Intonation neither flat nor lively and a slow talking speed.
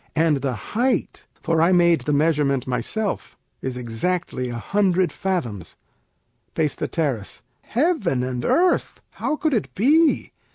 No: wide, 7.6 semitones; slow, 125 wpm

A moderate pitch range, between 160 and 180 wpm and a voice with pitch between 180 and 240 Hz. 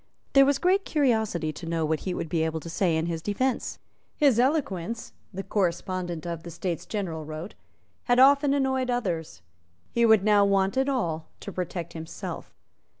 No: wide, 7.1 semitones; average, 175 wpm; high, 190 Hz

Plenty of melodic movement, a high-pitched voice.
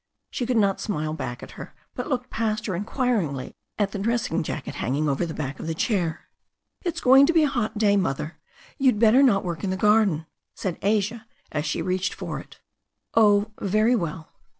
Yes: wide, 5.8 semitones; high, 200 Hz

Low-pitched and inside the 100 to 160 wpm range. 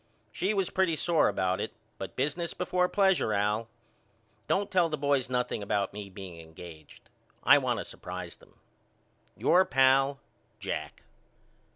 Yes: low, 130 Hz; average, 145 wpm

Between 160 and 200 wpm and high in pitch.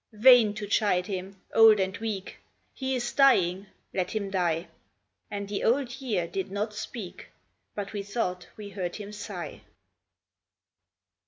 No: average, 145 wpm; high, 205 Hz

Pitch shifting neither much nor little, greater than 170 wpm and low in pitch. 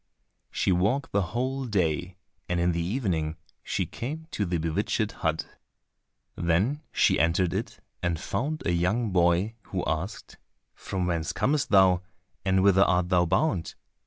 No: average, 4.7 semitones; average, 150 wpm; very low, 95 Hz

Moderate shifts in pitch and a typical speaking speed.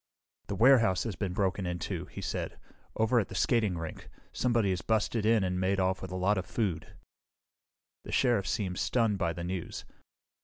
Yes: average, 3.5 semitones; average, 185 wpm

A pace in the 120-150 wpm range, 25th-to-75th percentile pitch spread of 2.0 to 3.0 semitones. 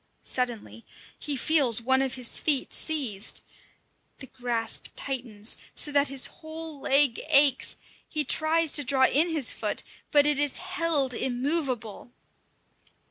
No: slow, 135 wpm; average, 3.6 semitones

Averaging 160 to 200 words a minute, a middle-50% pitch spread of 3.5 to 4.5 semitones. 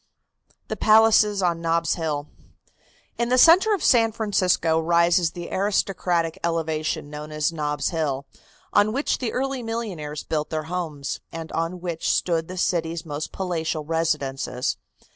No: average, 145 wpm; average, 4.2 semitones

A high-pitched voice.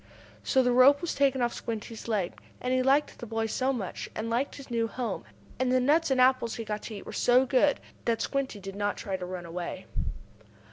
Yes: high, 240 Hz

